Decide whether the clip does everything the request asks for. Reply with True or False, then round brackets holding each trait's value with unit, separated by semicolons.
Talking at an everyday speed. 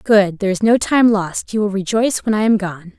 False (240 wpm)